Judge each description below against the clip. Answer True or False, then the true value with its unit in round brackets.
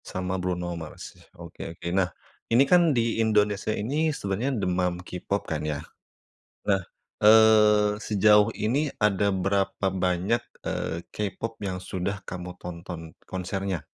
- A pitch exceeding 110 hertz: False (100 Hz)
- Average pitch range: True (3.0 semitones)